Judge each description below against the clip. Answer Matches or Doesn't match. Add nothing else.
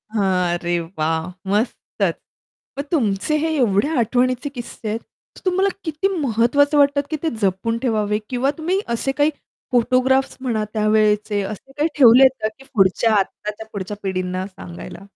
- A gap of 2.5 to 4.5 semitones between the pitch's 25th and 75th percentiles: Doesn't match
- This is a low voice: Doesn't match